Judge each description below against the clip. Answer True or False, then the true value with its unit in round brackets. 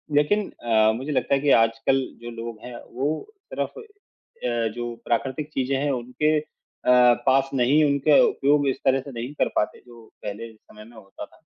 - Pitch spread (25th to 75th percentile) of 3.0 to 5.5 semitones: True (3.4 semitones)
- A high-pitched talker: False (130 Hz)